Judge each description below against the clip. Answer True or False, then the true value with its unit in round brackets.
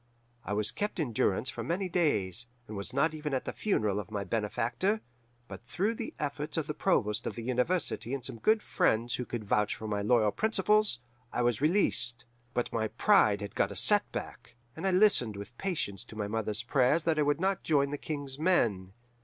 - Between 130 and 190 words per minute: False (205 wpm)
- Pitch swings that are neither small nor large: False (8.0 semitones)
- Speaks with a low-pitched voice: True (125 Hz)